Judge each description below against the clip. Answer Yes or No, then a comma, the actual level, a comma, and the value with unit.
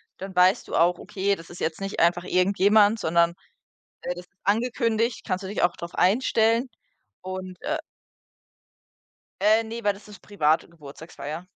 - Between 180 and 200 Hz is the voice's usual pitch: Yes, high, 190 Hz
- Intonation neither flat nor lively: Yes, average, 3.7 semitones